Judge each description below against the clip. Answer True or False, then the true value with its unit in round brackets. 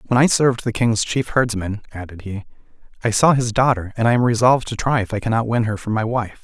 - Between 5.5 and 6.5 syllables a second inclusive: True (6.1 syllables/s)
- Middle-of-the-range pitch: False (115 Hz)